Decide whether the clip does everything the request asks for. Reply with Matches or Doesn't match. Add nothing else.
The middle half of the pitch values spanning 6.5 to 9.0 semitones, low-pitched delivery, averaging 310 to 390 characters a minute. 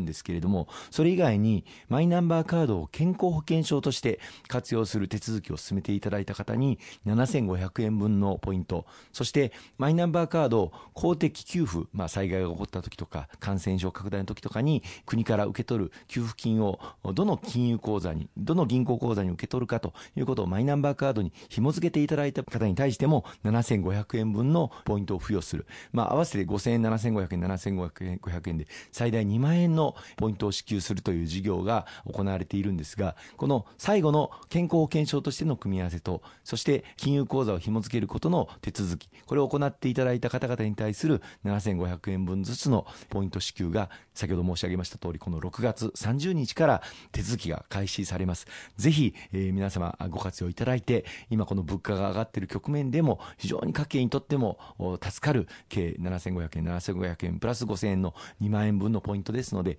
Doesn't match